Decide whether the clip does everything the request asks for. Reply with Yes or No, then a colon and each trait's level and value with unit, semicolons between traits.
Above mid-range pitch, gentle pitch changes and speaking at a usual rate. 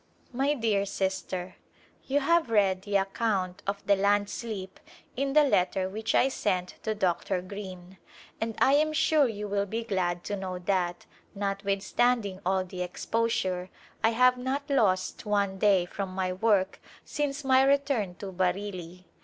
No: high, 200 Hz; average, 3.8 semitones; average, 160 wpm